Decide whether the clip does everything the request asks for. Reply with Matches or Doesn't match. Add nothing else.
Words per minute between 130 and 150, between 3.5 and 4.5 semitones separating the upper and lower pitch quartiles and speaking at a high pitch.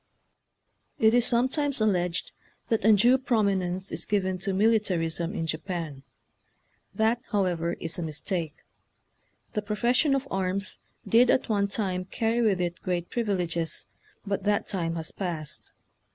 Matches